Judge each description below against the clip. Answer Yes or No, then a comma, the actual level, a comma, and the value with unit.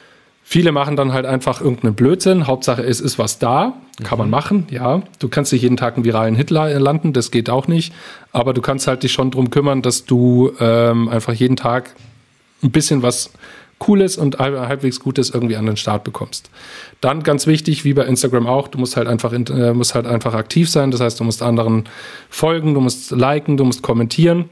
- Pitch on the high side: No, low, 130 Hz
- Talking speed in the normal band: No, fast, 205 wpm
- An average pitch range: Yes, average, 3.2 semitones